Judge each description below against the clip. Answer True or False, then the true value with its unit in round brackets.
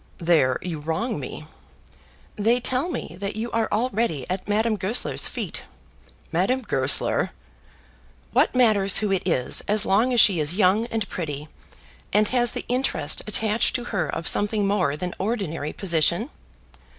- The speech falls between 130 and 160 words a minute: True (150 wpm)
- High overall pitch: True (200 Hz)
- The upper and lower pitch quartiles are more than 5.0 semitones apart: True (5.4 semitones)